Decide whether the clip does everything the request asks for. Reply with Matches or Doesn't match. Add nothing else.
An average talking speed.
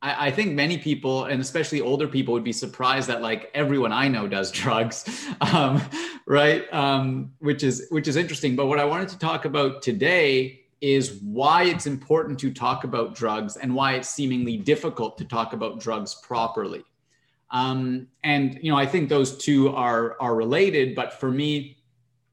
Matches